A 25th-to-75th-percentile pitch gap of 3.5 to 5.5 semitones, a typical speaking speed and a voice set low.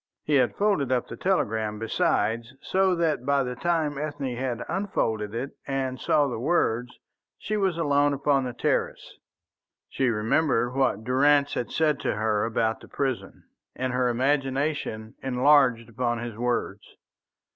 Yes: average, 3.8 semitones; average, 150 wpm; low, 130 Hz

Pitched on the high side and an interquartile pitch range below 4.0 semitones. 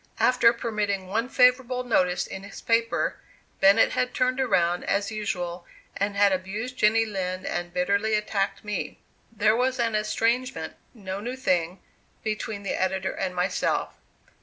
Yes: high, 210 Hz; average, 3.6 semitones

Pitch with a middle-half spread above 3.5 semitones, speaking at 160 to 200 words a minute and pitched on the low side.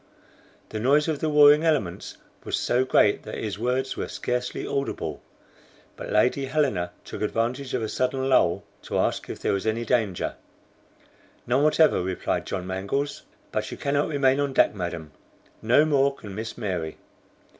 Yes: wide, 5.5 semitones; average, 165 wpm; low, 125 Hz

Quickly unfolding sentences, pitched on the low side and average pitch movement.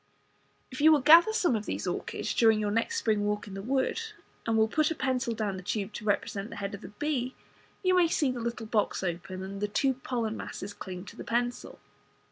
No: fast, 230 wpm; high, 225 Hz; average, 4.6 semitones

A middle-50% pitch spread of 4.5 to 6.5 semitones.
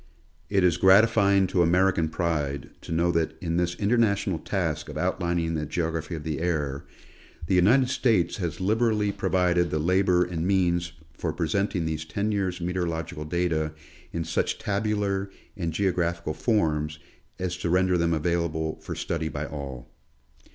No: average, 3.1 semitones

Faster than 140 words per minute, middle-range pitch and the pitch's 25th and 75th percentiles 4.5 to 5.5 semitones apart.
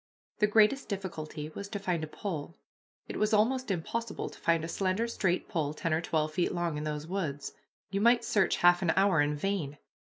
Yes: average, 200 wpm; medium, 180 Hz; average, 4.9 semitones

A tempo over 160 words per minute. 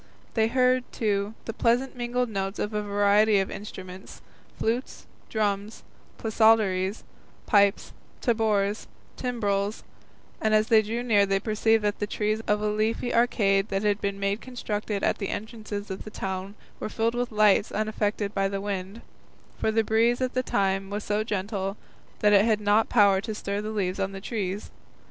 Yes: average, 170 wpm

